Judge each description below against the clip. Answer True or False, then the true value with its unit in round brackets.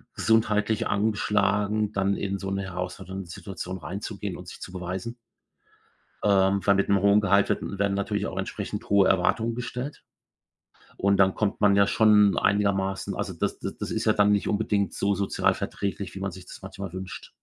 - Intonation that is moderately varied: False (1.3 semitones)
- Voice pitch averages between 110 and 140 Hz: False (100 Hz)